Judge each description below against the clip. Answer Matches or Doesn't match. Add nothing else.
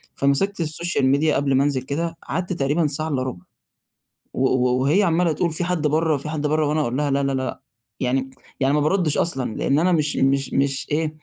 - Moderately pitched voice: Matches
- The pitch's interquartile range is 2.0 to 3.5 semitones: Matches